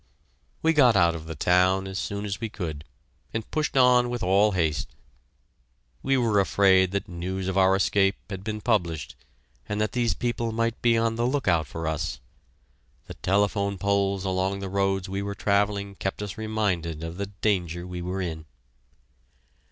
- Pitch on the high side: No, low, 100 Hz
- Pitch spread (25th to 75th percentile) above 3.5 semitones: No, average, 2.9 semitones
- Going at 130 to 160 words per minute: No, average, 175 wpm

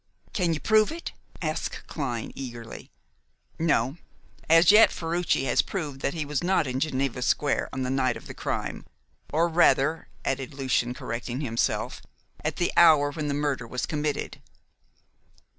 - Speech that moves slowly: No, average, 155 wpm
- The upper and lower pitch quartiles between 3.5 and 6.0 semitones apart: Yes, average, 4.0 semitones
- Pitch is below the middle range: No, medium, 145 Hz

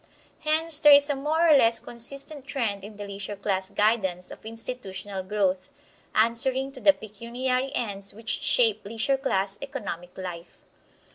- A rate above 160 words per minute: No, average, 150 wpm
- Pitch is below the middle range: No, high, 225 Hz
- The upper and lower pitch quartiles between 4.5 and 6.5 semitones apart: Yes, wide, 5.4 semitones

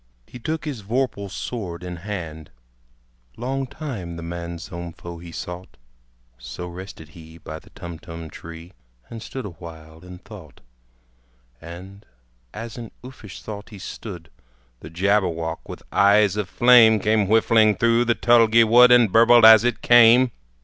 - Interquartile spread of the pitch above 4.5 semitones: Yes, average, 5.2 semitones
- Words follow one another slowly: No, average, 145 wpm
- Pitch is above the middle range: No, low, 100 Hz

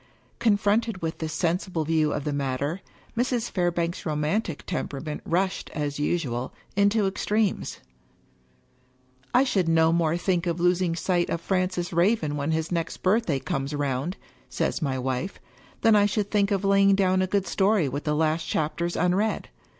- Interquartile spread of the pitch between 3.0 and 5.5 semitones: Yes, average, 4.4 semitones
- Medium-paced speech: Yes, average, 165 wpm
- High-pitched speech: No, medium, 175 Hz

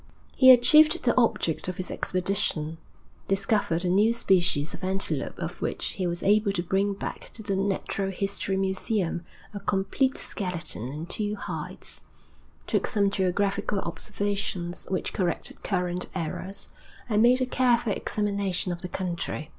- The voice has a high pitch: Yes, high, 195 Hz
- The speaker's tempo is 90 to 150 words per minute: Yes, average, 145 wpm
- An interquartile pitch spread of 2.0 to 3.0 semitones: Yes, narrow, 2.6 semitones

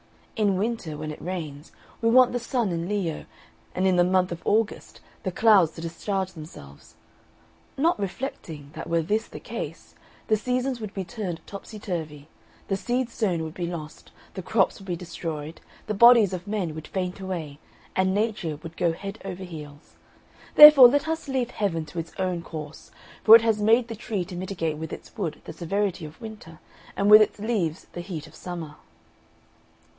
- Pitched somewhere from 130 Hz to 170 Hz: No, medium, 185 Hz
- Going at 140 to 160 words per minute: No, average, 185 wpm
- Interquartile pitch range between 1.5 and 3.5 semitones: No, average, 4.7 semitones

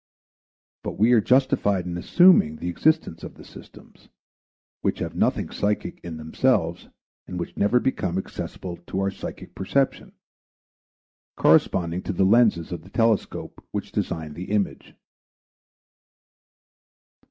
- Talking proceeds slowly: Yes, slow, 130 wpm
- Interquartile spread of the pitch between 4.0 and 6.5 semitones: Yes, average, 5.2 semitones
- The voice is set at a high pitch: No, very low, 95 Hz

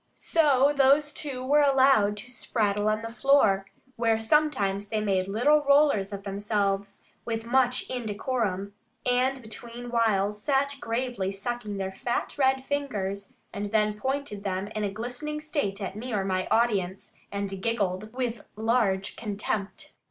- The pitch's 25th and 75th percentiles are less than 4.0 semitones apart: No, average, 4.5 semitones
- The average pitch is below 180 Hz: No, high, 225 Hz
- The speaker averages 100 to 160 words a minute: Yes, average, 150 wpm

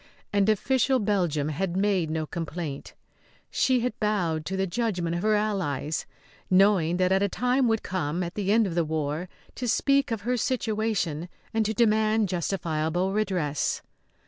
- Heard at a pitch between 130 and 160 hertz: No, high, 190 Hz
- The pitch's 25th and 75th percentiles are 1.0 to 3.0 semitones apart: No, average, 4.5 semitones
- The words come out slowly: No, average, 160 wpm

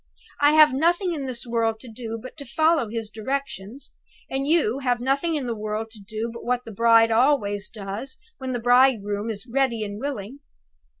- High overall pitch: Yes, high, 235 Hz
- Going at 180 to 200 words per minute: Yes, average, 190 wpm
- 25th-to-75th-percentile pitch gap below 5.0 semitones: Yes, average, 3.8 semitones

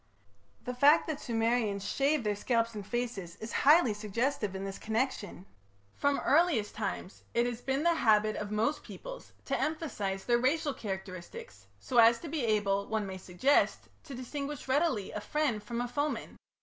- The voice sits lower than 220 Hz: No, high, 235 Hz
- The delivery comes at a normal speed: Yes, average, 175 wpm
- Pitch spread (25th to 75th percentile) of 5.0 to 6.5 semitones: Yes, wide, 5.4 semitones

